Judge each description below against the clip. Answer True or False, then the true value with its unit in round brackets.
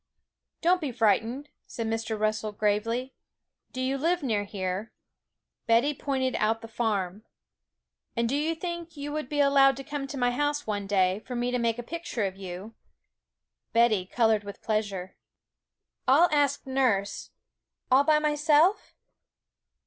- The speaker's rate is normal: True (150 wpm)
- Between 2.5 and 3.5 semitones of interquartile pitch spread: False (5.1 semitones)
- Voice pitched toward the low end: False (245 Hz)